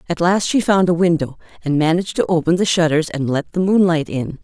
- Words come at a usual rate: No, fast, 230 wpm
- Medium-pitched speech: Yes, medium, 170 Hz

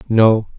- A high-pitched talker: No, low, 110 Hz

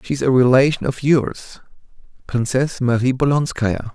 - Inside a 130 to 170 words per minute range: Yes, slow, 135 wpm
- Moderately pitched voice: No, low, 130 Hz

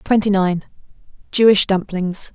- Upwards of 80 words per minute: No, slow, 75 wpm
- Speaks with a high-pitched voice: Yes, high, 195 Hz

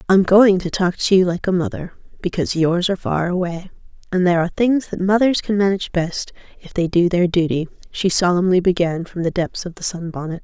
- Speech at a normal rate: No, fast, 215 wpm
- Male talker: No, female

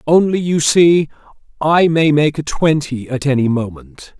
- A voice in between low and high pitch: Yes, medium, 145 Hz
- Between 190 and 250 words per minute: No, average, 155 wpm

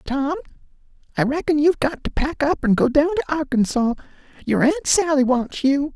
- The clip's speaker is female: No, male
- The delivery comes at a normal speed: Yes, average, 170 wpm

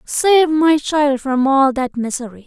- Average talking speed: Yes, average, 170 wpm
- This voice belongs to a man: No, female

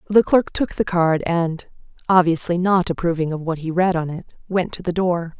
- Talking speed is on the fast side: Yes, fast, 210 wpm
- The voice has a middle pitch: Yes, medium, 175 Hz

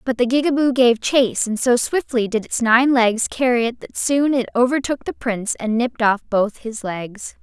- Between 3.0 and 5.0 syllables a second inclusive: Yes, 4.9 syllables/s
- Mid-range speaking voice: No, high, 240 Hz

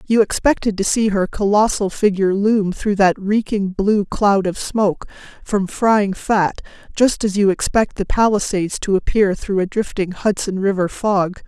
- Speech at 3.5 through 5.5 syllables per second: Yes, 4.5 syllables/s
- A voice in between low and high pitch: No, high, 200 Hz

